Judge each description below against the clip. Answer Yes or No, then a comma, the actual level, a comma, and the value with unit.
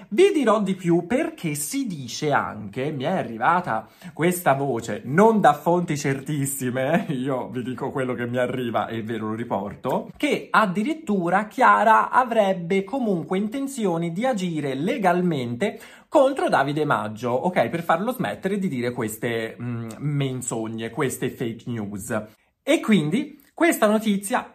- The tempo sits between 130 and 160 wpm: Yes, average, 135 wpm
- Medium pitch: Yes, medium, 160 Hz